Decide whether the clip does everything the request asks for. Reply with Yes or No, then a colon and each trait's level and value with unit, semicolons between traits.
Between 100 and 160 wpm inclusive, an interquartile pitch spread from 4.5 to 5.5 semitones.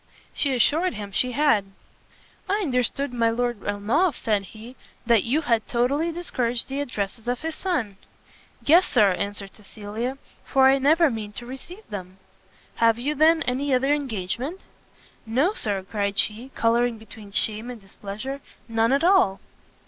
Yes: average, 155 wpm; average, 5.0 semitones